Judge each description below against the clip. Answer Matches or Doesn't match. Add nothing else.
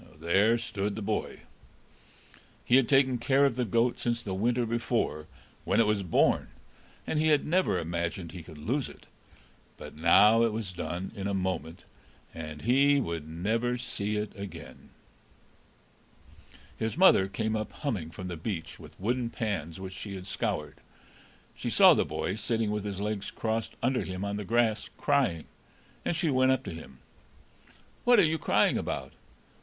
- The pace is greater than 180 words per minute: Doesn't match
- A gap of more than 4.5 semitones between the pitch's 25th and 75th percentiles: Matches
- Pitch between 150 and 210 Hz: Doesn't match